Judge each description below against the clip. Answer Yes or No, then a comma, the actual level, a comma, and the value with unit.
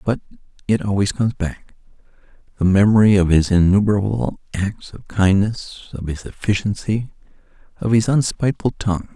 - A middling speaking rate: No, slow, 125 wpm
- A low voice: Yes, low, 100 Hz